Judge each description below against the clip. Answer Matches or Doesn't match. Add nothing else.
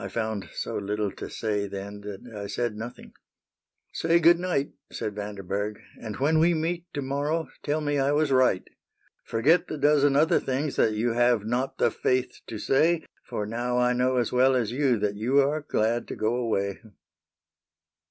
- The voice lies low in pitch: Matches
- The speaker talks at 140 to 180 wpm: Doesn't match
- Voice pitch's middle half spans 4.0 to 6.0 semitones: Matches